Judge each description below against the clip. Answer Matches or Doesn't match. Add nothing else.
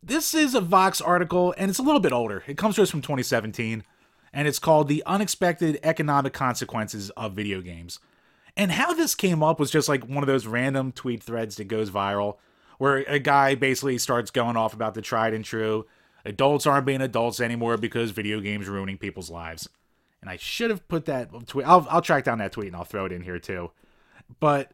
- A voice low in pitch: Matches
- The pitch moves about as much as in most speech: Doesn't match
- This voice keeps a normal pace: Doesn't match